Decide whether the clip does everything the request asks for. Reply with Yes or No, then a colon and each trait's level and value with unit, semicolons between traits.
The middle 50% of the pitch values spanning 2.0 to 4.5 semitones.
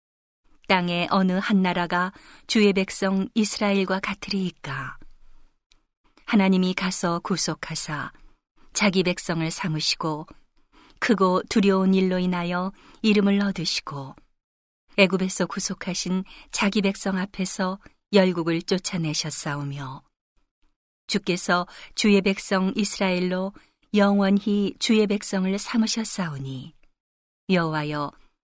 Yes: narrow, 2.4 semitones